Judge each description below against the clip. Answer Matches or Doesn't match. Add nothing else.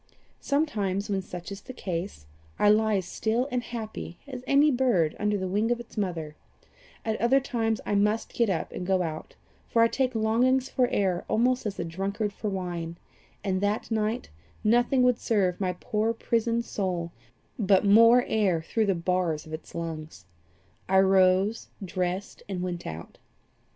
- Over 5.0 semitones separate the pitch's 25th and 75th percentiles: Doesn't match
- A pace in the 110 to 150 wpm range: Doesn't match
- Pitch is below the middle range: Doesn't match